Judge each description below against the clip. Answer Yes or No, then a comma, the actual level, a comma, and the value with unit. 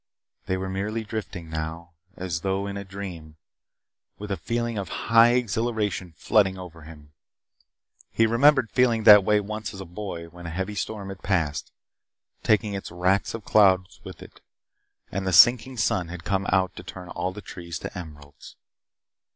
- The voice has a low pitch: Yes, very low, 95 Hz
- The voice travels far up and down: No, average, 3.5 semitones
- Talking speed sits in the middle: Yes, average, 170 wpm